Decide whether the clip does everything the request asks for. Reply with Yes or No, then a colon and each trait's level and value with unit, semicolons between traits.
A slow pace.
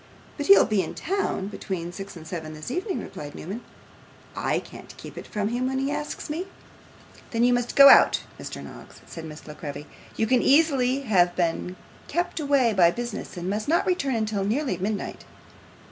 No: average, 190 wpm